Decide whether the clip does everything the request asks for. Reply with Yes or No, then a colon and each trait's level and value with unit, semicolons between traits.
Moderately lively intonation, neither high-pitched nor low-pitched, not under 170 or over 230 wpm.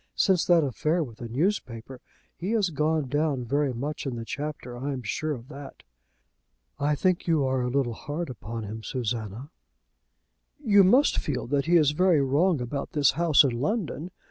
Yes: average, 4.7 semitones; medium, 145 Hz; average, 180 wpm